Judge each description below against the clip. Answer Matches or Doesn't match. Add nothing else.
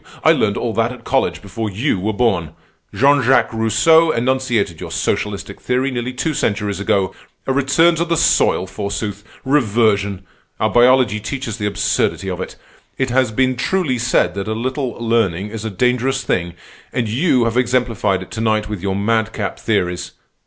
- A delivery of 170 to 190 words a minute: Matches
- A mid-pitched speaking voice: Doesn't match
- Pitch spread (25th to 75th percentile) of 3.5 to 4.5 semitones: Matches